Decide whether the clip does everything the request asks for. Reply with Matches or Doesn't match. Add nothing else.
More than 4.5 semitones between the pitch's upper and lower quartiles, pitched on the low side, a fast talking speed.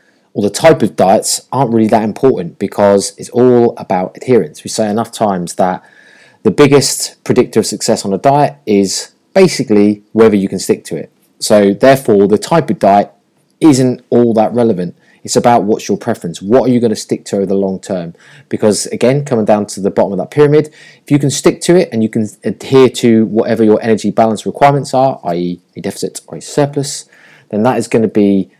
Matches